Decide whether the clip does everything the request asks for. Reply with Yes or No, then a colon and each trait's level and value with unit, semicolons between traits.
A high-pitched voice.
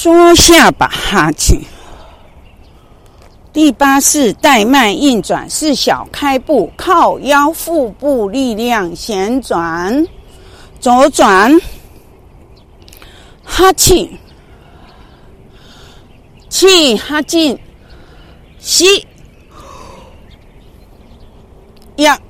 Yes: very high, 290 Hz